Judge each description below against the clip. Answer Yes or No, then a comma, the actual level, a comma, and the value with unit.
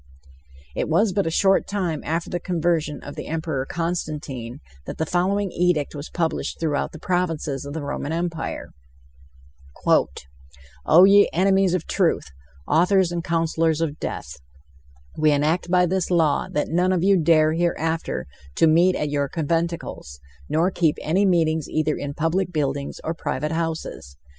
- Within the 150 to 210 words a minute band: Yes, average, 155 wpm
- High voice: No, medium, 165 Hz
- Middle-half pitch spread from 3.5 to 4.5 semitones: No, average, 2.9 semitones